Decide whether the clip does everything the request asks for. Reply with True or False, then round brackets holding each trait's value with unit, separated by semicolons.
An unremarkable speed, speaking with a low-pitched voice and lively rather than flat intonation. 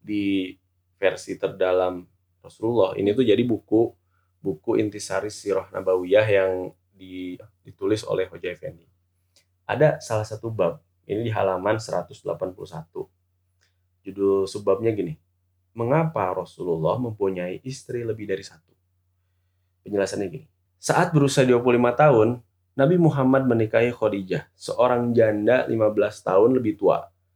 False (115 wpm; 100 Hz; 4.4 semitones)